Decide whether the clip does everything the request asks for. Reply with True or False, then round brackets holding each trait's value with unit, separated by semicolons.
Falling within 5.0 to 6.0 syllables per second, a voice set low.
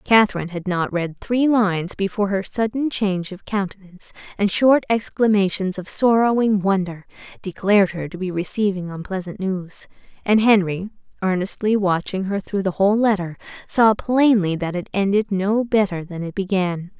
False (5.1 syllables/s; 195 Hz)